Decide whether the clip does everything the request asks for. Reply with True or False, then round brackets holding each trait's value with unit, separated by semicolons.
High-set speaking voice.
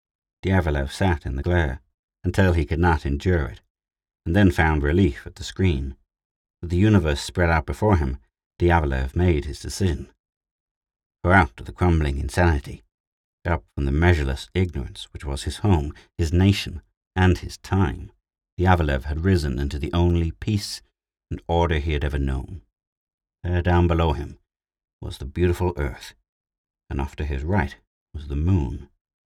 False (85 Hz)